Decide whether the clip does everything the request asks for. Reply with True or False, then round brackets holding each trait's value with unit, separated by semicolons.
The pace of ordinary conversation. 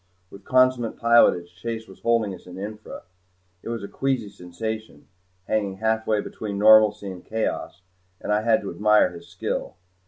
True (160 wpm)